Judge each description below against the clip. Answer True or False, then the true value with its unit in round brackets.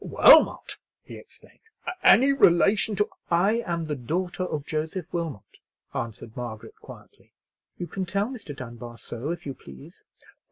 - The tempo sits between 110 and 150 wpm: True (145 wpm)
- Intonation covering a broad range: True (7.2 semitones)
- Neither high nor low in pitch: True (170 Hz)